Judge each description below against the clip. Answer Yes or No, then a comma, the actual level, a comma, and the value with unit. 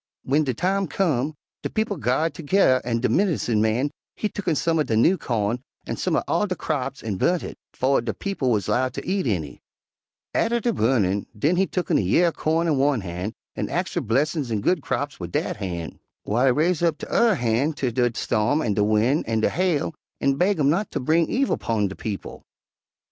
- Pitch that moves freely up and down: Yes, wide, 7.2 semitones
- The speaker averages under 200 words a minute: No, fast, 220 wpm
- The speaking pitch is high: No, low, 135 Hz